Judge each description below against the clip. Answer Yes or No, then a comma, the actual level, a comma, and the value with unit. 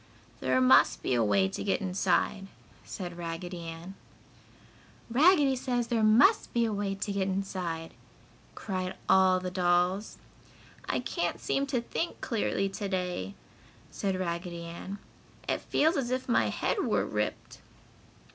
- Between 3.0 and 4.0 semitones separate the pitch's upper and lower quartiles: No, average, 4.4 semitones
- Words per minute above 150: No, average, 145 wpm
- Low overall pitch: No, high, 190 Hz